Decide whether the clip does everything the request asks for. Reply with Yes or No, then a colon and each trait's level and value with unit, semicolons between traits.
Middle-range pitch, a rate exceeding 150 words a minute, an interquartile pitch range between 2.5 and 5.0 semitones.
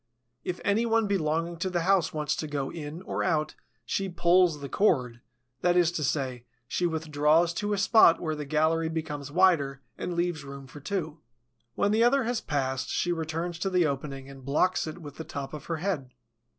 Yes: medium, 160 Hz; average, 200 wpm; average, 3.6 semitones